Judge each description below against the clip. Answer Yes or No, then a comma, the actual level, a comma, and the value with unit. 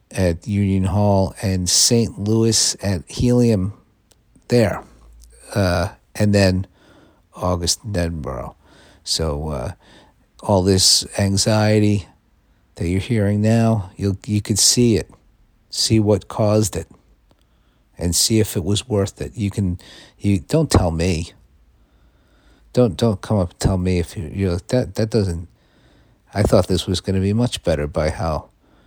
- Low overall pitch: Yes, low, 100 Hz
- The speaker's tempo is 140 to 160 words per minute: Yes, average, 150 wpm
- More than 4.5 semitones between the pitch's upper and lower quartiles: No, average, 3.7 semitones